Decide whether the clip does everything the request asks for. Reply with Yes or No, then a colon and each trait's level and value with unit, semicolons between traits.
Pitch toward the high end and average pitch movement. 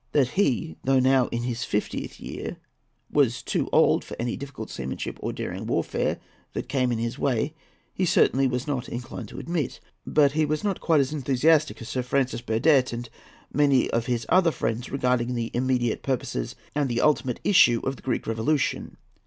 No: low, 130 Hz; average, 3.3 semitones